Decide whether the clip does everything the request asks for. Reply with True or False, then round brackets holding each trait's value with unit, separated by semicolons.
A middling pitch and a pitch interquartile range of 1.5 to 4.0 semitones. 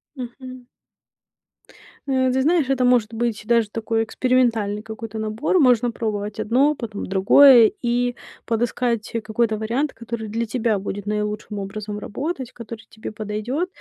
False (230 Hz; 2.8 semitones)